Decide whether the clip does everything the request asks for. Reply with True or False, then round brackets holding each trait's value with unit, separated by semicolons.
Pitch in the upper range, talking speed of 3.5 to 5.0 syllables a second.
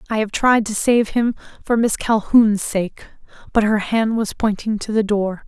True (215 Hz; 4.7 syllables/s)